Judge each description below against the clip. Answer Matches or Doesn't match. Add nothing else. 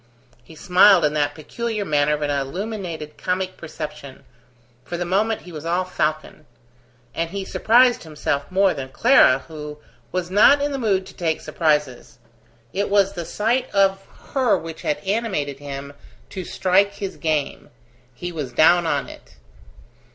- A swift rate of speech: Doesn't match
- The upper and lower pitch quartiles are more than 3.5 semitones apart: Matches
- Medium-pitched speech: Matches